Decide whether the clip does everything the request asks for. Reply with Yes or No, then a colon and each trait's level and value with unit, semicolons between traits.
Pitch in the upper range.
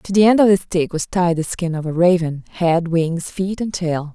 No: medium, 175 Hz